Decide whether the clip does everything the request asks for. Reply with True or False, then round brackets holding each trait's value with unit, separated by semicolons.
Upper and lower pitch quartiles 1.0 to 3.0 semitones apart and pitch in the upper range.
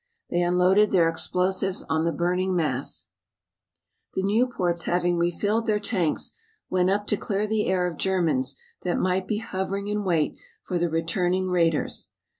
False (2.4 semitones; 180 Hz)